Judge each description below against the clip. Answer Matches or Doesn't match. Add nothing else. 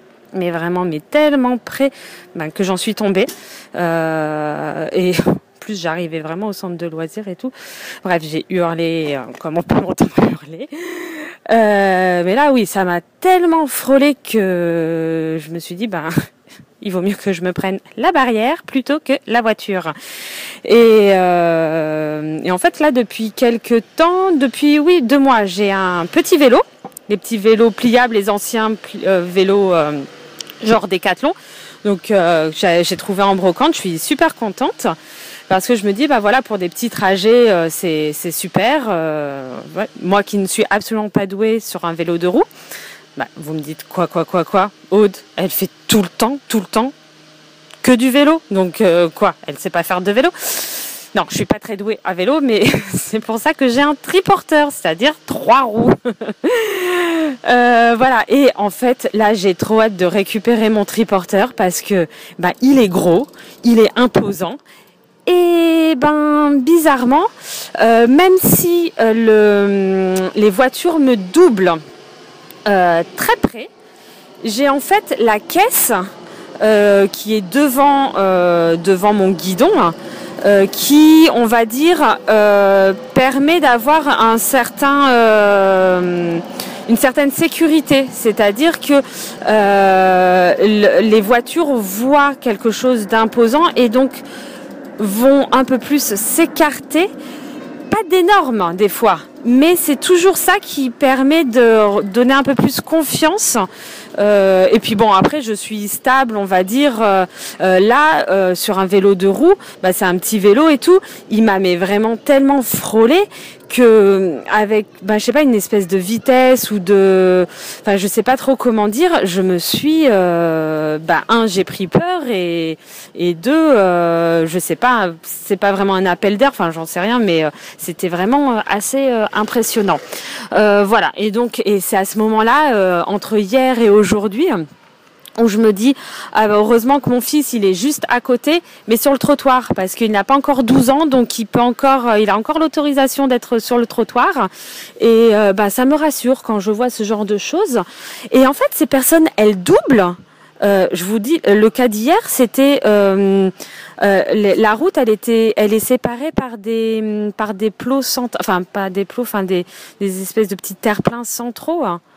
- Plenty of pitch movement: Matches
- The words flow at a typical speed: Matches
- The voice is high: Matches